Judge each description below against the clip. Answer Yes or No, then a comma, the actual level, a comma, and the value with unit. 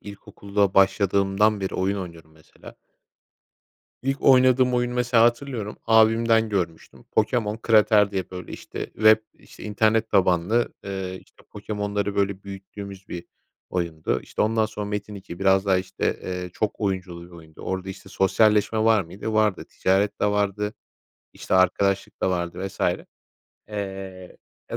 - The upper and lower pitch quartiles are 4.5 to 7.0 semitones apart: No, narrow, 2.5 semitones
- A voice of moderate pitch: No, low, 100 Hz